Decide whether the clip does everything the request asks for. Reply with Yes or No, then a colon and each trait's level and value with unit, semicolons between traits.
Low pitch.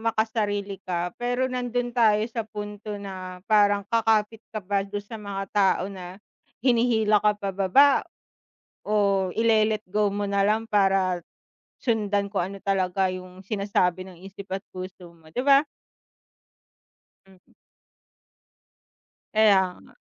No: high, 205 Hz